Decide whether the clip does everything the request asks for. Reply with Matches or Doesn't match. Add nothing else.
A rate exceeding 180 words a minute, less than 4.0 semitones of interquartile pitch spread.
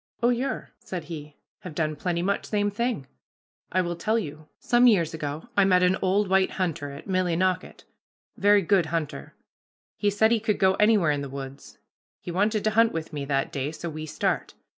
Doesn't match